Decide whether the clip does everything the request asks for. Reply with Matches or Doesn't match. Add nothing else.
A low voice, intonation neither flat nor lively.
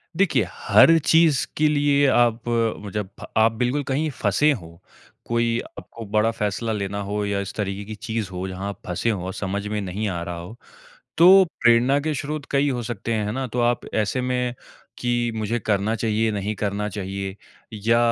Matches